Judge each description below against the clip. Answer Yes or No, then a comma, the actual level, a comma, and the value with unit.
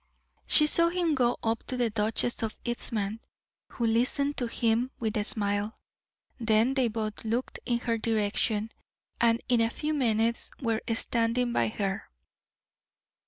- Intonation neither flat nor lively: No, narrow, 2.1 semitones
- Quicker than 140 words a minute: Yes, average, 150 wpm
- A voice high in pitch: Yes, high, 230 Hz